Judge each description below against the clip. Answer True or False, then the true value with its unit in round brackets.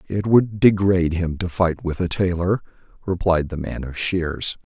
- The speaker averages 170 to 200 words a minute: True (175 wpm)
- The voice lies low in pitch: True (90 Hz)